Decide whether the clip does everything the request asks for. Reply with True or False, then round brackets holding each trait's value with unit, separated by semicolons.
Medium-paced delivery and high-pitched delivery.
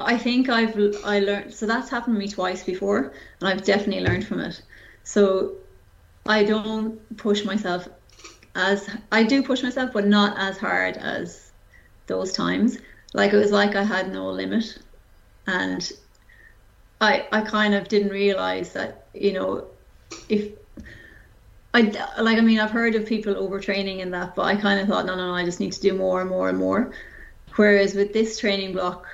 True (180 wpm; 205 Hz)